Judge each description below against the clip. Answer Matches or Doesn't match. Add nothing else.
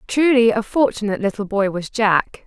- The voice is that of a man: Doesn't match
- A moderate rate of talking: Matches